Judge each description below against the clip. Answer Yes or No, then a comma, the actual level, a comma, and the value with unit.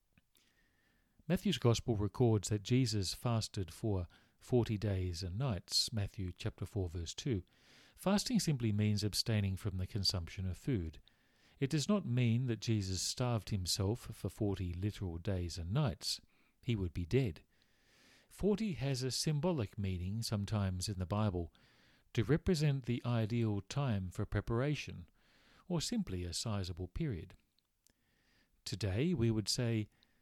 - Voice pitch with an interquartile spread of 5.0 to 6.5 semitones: No, average, 4.4 semitones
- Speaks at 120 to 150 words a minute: Yes, slow, 135 wpm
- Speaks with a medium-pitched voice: No, low, 110 Hz